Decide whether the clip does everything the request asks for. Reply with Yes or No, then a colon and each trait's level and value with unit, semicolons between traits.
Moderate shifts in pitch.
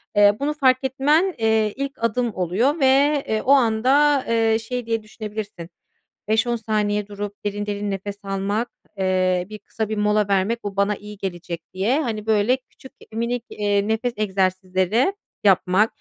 Yes: average, 3.2 semitones